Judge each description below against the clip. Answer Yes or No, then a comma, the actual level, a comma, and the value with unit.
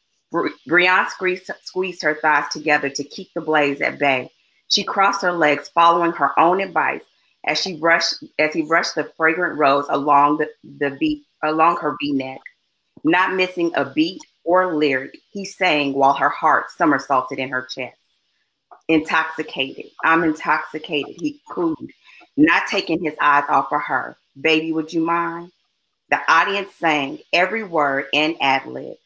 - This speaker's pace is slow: No, average, 155 wpm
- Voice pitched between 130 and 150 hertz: No, medium, 160 Hz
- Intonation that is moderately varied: Yes, average, 4.1 semitones